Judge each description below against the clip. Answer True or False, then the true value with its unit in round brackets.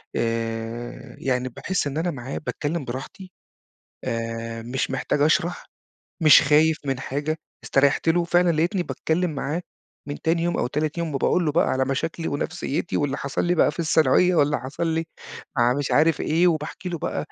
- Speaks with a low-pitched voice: False (150 Hz)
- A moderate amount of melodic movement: True (4.0 semitones)